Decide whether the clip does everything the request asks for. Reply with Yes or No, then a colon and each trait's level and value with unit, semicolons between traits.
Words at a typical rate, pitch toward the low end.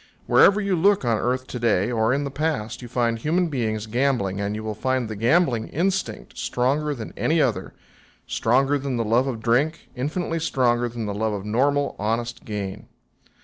Yes: average, 190 wpm; low, 125 Hz